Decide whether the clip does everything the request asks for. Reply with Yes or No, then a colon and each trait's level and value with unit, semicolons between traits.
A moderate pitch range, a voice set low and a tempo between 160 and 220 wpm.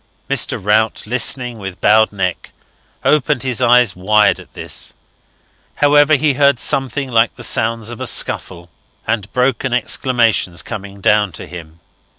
No: average, 4.2 semitones; low, 115 Hz; average, 145 wpm